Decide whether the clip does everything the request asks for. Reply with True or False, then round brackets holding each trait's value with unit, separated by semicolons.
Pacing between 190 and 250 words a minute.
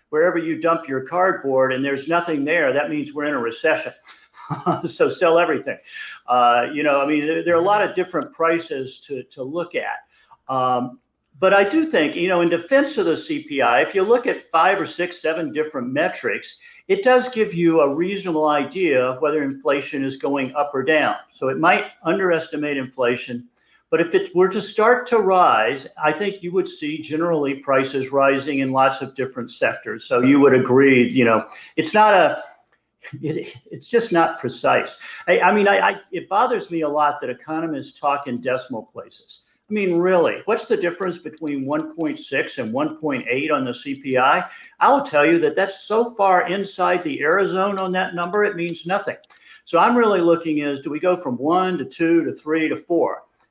True (195 wpm)